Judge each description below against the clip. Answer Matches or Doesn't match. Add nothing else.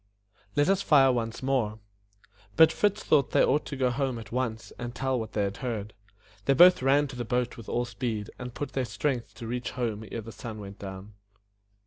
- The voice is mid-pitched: Doesn't match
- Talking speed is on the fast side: Matches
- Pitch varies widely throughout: Doesn't match